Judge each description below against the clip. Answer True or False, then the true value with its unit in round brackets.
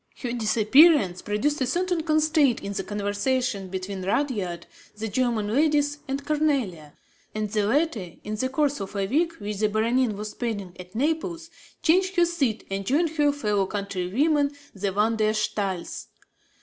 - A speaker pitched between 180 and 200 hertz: False (230 Hz)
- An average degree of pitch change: False (6.5 semitones)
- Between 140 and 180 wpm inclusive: True (160 wpm)